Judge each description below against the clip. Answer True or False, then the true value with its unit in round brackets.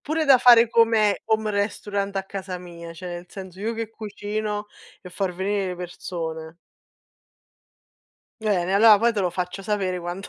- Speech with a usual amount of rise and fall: True (3.1 semitones)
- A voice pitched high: True (200 Hz)